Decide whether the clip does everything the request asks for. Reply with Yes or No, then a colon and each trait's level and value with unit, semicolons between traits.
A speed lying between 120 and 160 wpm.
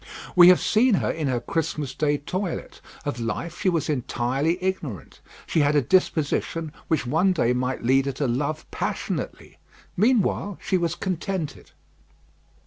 Yes: average, 150 wpm